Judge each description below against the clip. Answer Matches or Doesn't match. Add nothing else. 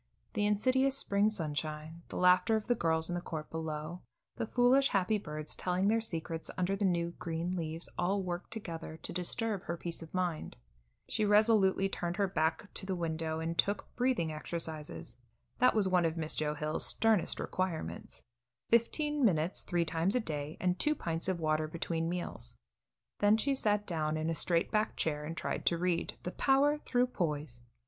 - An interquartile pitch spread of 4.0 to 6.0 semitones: Matches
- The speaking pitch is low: Doesn't match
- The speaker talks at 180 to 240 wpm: Matches